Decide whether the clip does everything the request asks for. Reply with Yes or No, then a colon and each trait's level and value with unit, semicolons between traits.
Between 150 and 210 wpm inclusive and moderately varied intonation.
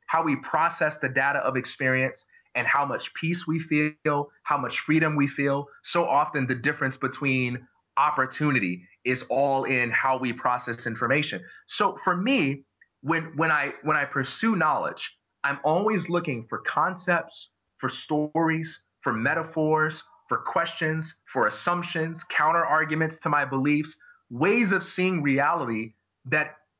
No: average, 140 wpm; average, 3.5 semitones